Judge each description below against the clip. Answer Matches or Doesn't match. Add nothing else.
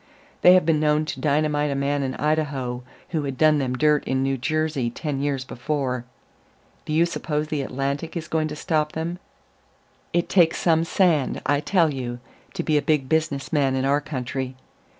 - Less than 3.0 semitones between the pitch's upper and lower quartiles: Matches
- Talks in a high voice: Doesn't match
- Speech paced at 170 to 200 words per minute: Matches